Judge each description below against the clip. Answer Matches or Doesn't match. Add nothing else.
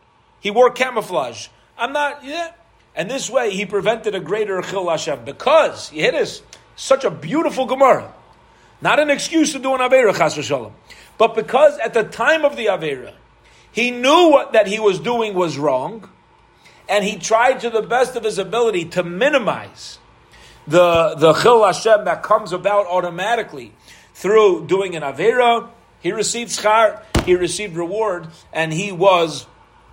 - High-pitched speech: Matches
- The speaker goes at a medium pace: Matches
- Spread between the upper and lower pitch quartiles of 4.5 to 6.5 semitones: Matches